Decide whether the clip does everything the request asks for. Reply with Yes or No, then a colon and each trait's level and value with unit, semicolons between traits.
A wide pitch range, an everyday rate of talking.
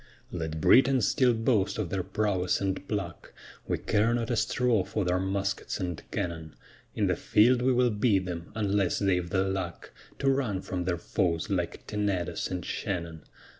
No: average, 3.7 semitones; average, 170 wpm